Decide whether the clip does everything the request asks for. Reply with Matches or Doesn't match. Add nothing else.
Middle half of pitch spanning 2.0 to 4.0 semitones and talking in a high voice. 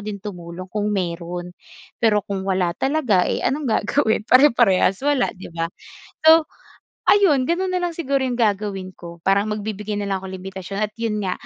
Doesn't match